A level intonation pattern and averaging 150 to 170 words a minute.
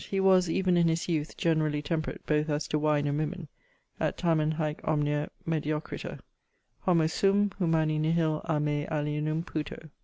Yes: narrow, 1.8 semitones; average, 165 wpm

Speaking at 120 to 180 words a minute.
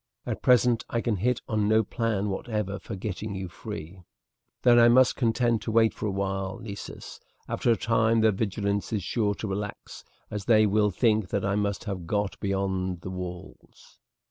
No: average, 190 wpm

